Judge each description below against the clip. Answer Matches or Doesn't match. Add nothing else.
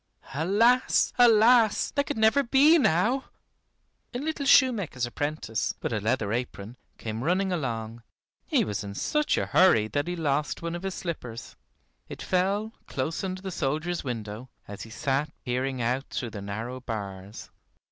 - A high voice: Doesn't match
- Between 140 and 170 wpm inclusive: Matches